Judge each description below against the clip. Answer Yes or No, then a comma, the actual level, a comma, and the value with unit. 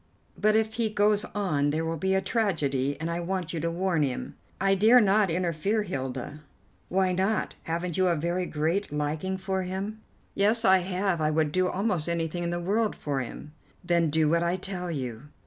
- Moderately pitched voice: Yes, medium, 180 Hz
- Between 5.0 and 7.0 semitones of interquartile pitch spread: No, average, 3.6 semitones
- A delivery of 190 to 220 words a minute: Yes, average, 200 wpm